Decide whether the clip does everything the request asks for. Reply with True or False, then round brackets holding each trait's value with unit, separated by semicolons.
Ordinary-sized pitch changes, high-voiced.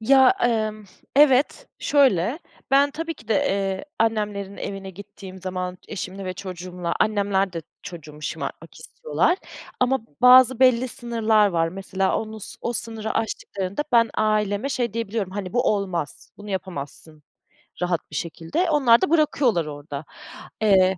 True (4.5 semitones; 205 Hz)